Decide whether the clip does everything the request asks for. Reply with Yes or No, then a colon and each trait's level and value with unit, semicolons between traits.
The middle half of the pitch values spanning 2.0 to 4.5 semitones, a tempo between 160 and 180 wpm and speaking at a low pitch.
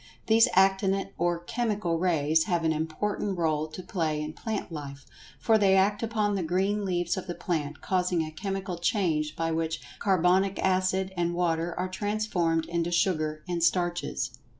No: average, 3.0 semitones; average, 165 wpm; medium, 175 Hz